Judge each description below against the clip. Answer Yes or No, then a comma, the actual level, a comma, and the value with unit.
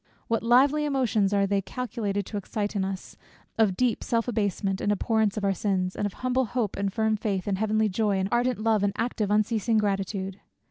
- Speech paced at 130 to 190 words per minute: No, average, 200 wpm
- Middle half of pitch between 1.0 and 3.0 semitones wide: Yes, narrow, 2.6 semitones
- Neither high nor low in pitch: No, high, 210 Hz